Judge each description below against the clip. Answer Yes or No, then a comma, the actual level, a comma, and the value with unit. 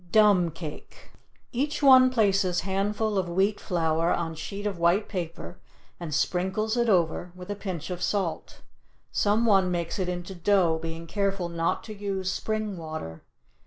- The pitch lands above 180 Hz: Yes, high, 190 Hz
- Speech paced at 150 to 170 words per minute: Yes, average, 160 wpm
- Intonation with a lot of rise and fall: No, average, 3.3 semitones